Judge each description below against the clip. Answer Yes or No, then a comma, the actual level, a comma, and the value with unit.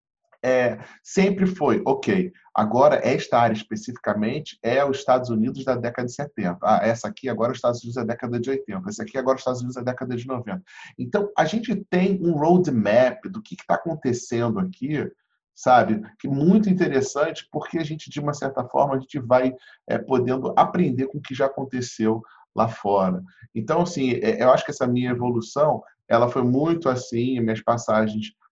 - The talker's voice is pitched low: Yes, low, 130 Hz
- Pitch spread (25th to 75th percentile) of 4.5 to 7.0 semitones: Yes, average, 4.8 semitones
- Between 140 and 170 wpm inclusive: No, fast, 185 wpm